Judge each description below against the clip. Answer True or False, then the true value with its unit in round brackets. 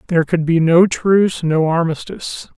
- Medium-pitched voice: True (170 Hz)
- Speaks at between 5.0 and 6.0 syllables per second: True (5.1 syllables/s)